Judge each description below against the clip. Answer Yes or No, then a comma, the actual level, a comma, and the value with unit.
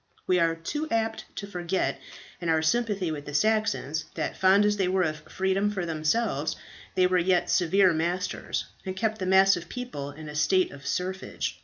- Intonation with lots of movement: No, average, 3.8 semitones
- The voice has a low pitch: No, medium, 185 Hz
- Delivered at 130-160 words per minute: No, average, 195 wpm